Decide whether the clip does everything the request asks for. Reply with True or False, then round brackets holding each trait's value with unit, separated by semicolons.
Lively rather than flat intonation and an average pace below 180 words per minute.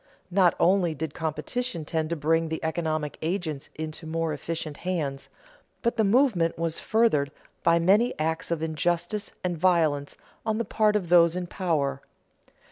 False (2.8 semitones; 155 wpm)